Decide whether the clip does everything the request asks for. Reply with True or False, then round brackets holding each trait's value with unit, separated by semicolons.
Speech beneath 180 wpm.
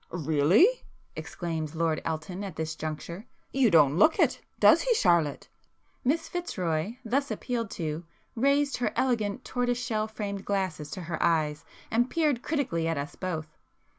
True (145 wpm)